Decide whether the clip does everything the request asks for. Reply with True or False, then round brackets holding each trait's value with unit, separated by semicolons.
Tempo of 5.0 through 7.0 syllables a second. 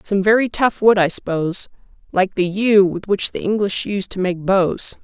False (4.7 syllables/s)